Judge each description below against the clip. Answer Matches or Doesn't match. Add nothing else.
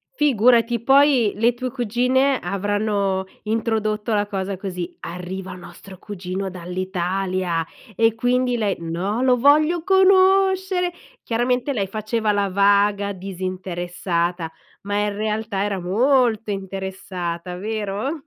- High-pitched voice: Matches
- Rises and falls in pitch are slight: Doesn't match